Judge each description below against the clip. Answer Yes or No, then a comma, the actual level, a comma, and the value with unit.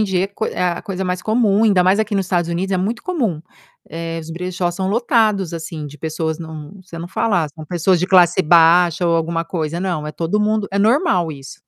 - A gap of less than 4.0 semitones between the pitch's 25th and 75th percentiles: Yes, average, 3.2 semitones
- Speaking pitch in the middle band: Yes, medium, 180 Hz